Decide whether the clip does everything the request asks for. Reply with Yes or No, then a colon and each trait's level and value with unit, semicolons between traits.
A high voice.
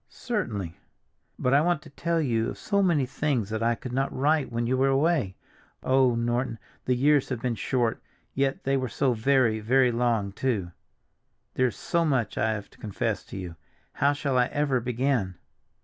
No: low, 125 Hz